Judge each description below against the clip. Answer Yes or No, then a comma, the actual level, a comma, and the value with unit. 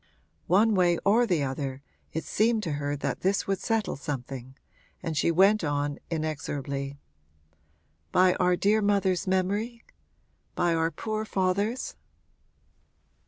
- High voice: No, medium, 180 Hz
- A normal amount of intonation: No, wide, 5.9 semitones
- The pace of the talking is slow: Yes, slow, 125 wpm